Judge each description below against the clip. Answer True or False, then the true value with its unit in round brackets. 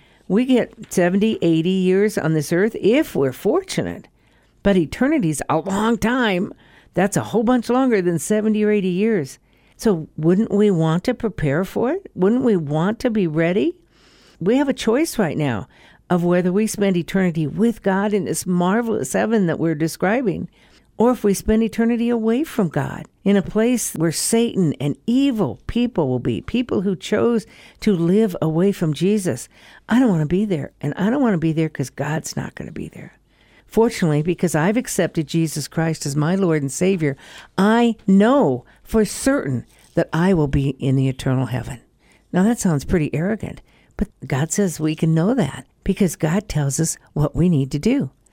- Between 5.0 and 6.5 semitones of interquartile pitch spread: True (5.6 semitones)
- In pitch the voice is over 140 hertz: True (185 Hz)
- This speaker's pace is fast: False (185 wpm)